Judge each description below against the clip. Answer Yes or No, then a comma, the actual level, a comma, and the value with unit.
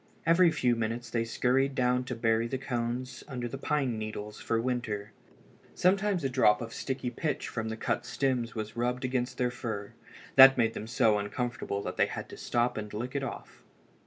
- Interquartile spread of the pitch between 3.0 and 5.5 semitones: No, narrow, 2.5 semitones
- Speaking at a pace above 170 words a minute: Yes, average, 195 wpm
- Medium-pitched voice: No, low, 120 Hz